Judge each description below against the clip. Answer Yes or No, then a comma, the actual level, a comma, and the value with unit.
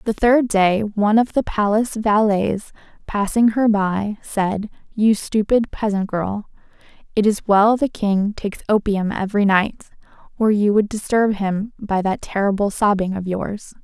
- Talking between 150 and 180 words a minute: Yes, average, 155 wpm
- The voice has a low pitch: No, high, 205 Hz